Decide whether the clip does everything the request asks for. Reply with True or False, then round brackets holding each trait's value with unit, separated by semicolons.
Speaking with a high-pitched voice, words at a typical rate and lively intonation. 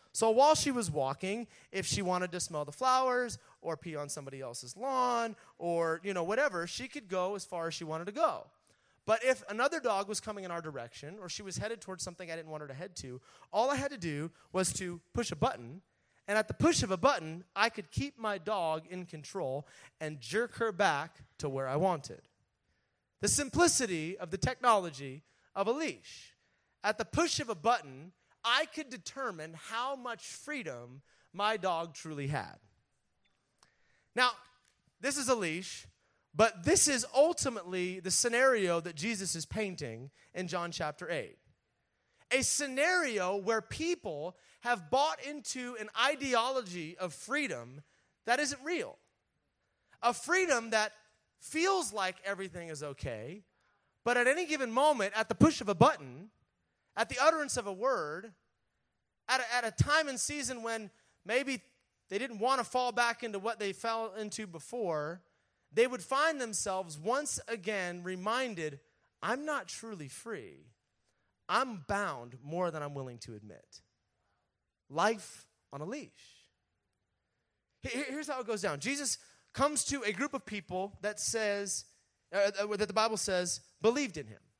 True (205 Hz; 165 wpm; 7.3 semitones)